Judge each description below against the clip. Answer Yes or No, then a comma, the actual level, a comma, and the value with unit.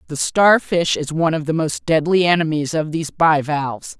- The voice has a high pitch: No, medium, 160 Hz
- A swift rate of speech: No, average, 180 wpm